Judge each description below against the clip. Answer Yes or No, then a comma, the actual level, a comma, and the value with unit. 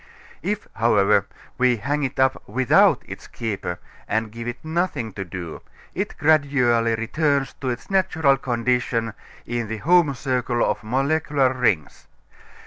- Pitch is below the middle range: Yes, low, 125 Hz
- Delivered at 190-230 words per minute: No, slow, 135 wpm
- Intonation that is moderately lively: Yes, average, 3.8 semitones